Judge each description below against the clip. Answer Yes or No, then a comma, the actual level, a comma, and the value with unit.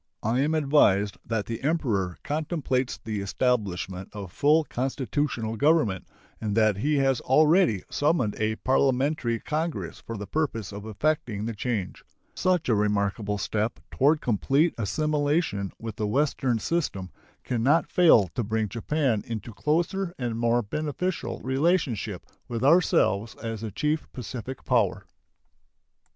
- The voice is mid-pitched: No, low, 120 Hz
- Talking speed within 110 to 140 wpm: Yes, slow, 135 wpm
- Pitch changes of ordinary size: No, wide, 6.1 semitones